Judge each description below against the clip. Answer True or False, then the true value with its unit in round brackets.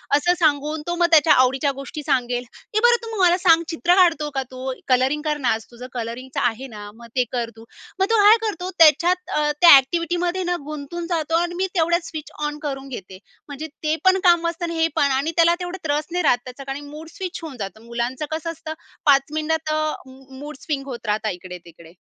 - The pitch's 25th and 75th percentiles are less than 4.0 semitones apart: False (4.7 semitones)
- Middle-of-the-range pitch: False (300 Hz)